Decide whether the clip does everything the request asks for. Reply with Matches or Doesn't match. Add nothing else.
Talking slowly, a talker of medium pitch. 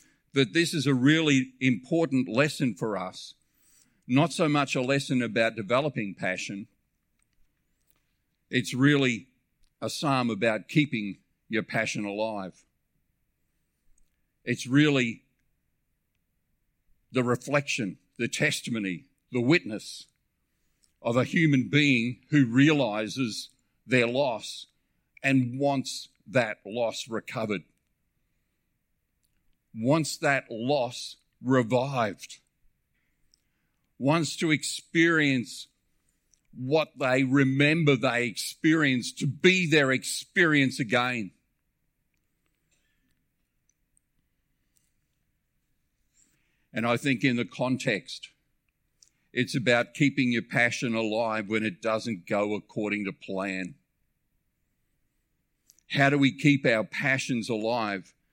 Doesn't match